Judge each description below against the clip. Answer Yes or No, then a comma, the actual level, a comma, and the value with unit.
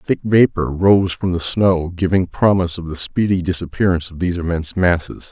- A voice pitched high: No, very low, 90 Hz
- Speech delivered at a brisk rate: No, average, 180 wpm